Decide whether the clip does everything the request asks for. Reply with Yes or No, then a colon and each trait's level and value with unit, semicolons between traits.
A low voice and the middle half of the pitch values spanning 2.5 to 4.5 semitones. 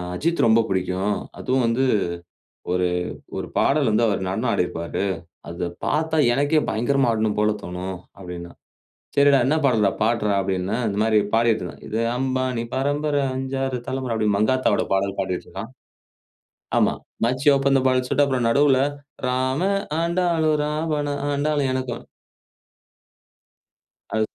No: low, 125 Hz; average, 5.0 semitones